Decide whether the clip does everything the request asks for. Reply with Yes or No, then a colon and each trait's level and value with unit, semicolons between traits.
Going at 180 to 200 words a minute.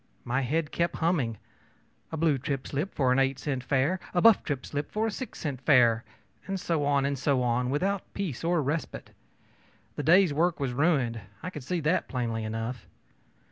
Yes: average, 190 wpm